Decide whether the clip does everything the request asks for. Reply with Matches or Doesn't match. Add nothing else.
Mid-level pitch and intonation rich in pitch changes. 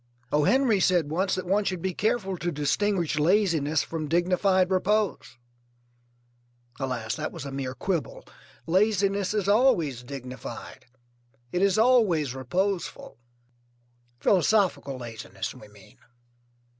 Matches